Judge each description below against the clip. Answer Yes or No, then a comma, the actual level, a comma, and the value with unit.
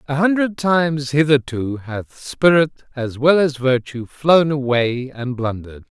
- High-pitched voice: No, medium, 140 Hz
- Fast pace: No, average, 140 wpm